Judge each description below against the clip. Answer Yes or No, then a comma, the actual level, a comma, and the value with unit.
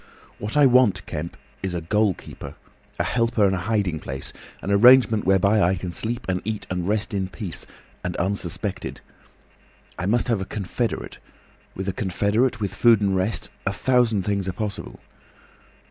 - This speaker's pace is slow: No, average, 165 wpm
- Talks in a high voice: No, low, 100 Hz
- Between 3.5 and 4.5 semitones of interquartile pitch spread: No, average, 3.1 semitones